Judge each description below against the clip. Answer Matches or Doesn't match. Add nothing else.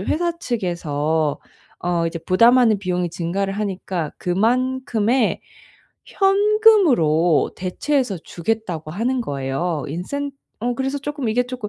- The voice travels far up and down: Matches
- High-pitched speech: Matches